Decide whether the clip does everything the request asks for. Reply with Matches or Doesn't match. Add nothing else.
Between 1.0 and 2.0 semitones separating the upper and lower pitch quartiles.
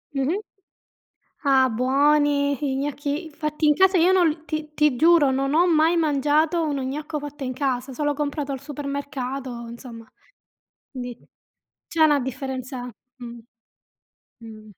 Doesn't match